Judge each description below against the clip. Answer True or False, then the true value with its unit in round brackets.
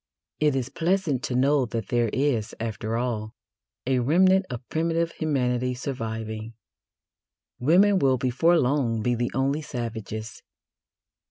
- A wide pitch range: False (4.5 semitones)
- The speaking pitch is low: True (125 Hz)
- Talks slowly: True (125 wpm)